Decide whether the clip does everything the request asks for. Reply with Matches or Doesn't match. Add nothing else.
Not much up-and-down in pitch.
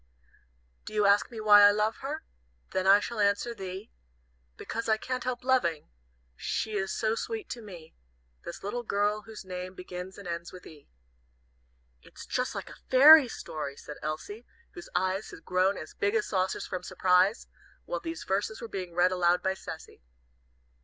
Doesn't match